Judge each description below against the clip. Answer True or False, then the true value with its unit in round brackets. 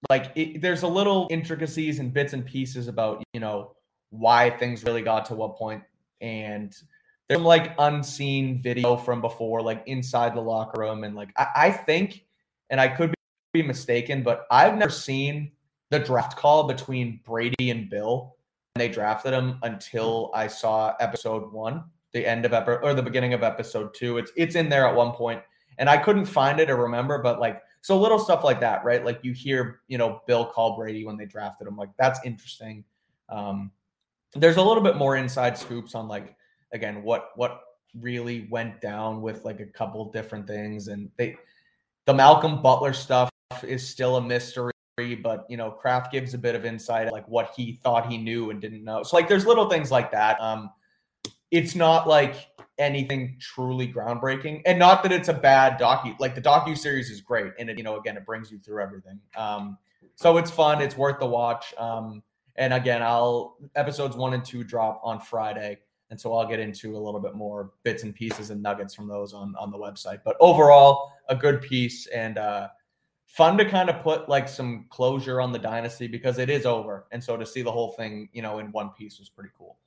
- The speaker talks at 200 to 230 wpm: True (205 wpm)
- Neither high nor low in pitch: False (120 Hz)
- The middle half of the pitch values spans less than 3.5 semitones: False (3.9 semitones)